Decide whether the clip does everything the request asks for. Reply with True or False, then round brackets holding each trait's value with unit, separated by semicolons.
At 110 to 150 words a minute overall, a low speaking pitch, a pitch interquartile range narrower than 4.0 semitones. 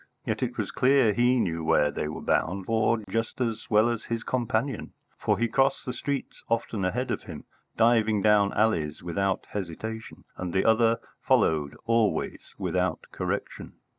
False (165 wpm; 110 Hz; 3.3 semitones)